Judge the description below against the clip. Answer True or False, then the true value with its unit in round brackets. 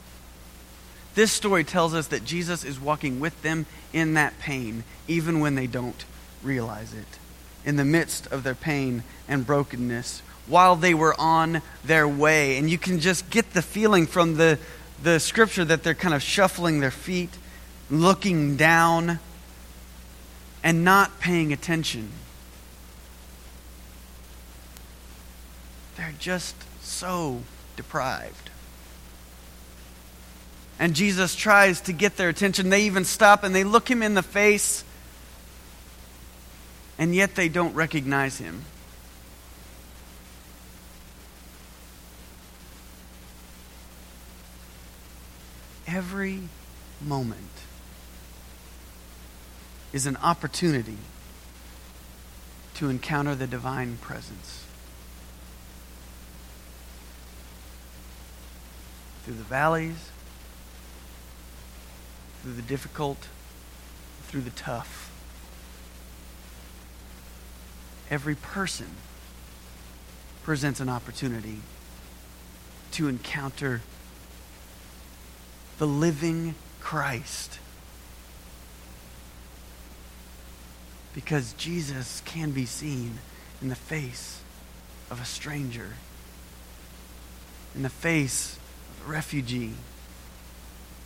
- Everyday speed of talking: False (85 wpm)